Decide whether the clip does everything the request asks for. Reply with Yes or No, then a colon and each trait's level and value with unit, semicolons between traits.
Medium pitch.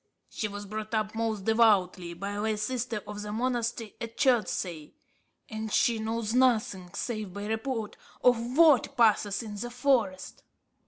No: high, 220 Hz